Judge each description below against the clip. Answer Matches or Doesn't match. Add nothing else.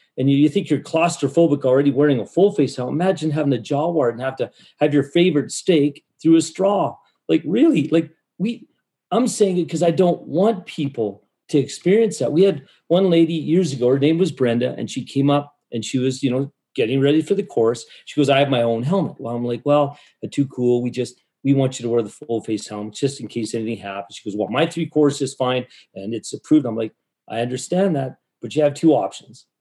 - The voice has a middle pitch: Matches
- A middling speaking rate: Doesn't match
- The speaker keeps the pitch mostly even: Doesn't match